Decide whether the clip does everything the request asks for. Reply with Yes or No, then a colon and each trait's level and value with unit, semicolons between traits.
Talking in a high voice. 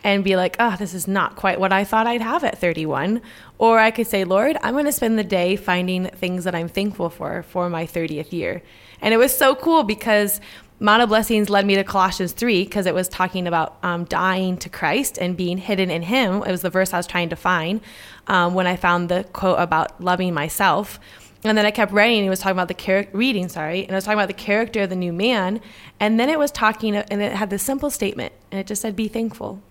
Yes: high, 195 Hz